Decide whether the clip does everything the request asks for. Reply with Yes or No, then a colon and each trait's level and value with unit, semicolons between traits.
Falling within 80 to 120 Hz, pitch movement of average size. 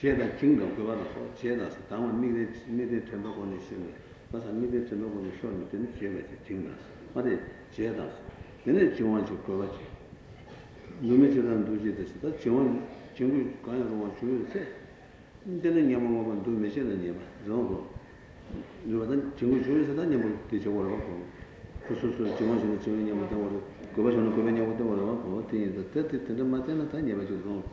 Yes: low, 115 Hz; average, 3.7 semitones